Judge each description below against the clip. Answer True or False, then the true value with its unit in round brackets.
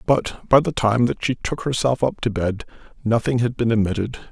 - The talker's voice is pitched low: True (120 Hz)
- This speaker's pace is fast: True (210 wpm)